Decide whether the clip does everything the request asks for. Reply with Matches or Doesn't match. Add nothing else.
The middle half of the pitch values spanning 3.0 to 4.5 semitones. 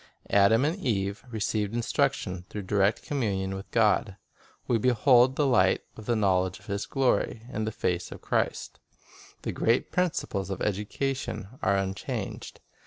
Matches